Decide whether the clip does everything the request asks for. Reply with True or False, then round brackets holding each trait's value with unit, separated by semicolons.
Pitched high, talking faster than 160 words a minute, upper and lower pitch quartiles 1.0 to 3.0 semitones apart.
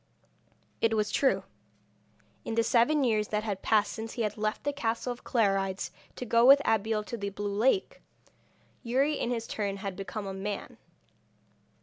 True (220 Hz; 170 wpm; 2.6 semitones)